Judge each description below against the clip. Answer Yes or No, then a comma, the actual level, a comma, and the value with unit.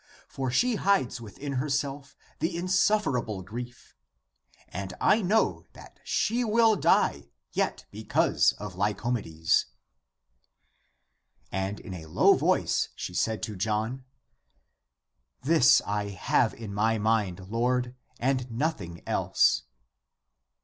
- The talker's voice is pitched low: Yes, low, 120 Hz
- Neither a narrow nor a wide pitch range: No, wide, 5.8 semitones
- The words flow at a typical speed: No, slow, 115 wpm